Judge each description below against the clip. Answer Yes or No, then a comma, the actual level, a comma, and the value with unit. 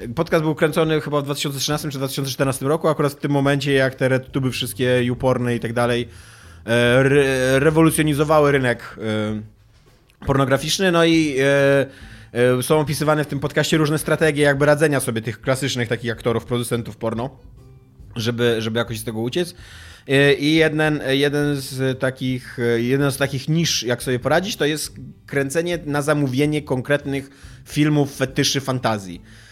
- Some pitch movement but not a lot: Yes, average, 3.6 semitones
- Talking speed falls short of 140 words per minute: No, average, 150 wpm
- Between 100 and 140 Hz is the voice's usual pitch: Yes, low, 135 Hz